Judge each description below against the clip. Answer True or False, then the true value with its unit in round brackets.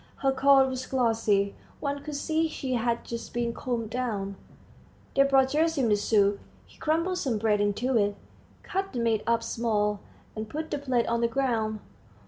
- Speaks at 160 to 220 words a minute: True (175 wpm)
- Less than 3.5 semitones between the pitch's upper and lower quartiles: False (4.0 semitones)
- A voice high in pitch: True (235 Hz)